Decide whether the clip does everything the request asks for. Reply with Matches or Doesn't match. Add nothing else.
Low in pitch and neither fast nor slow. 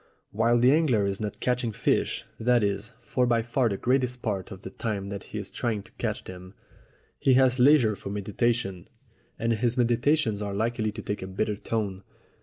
Matches